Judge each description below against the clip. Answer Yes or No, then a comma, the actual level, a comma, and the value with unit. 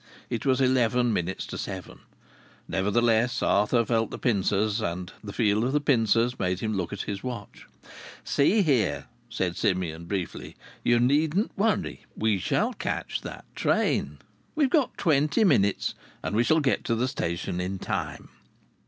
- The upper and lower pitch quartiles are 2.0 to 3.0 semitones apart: No, average, 5.1 semitones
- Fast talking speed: No, average, 155 wpm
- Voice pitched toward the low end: Yes, low, 115 Hz